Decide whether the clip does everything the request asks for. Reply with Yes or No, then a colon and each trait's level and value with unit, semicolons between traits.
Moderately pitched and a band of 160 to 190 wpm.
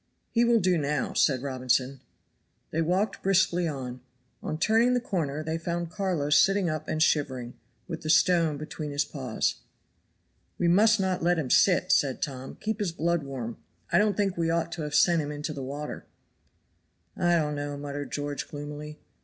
Yes: medium, 155 Hz; average, 180 wpm